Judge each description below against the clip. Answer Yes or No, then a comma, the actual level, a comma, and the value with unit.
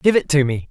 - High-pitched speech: No, medium, 150 Hz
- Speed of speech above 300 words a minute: Yes, fast, 340 wpm